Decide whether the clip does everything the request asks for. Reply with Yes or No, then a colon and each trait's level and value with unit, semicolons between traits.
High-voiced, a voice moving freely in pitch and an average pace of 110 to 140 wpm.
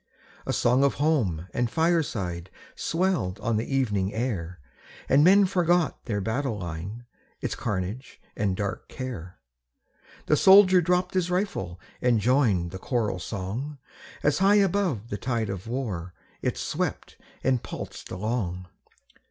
No: low, 120 Hz; wide, 8.2 semitones; slow, 135 wpm